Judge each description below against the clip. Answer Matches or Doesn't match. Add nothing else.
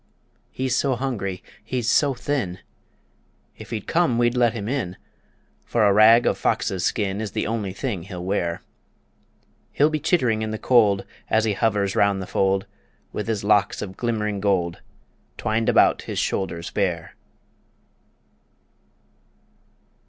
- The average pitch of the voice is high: Doesn't match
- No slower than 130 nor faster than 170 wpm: Matches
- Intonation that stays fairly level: Doesn't match